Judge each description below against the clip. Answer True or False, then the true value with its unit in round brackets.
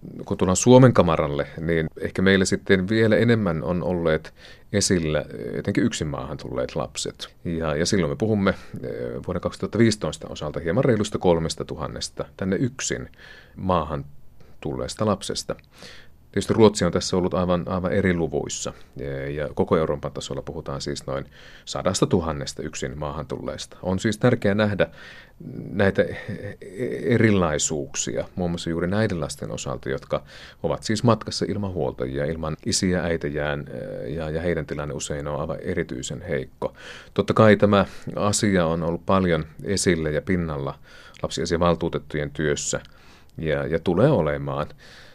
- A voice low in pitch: True (85 Hz)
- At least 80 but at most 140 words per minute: True (135 wpm)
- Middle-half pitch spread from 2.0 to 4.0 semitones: False (5.2 semitones)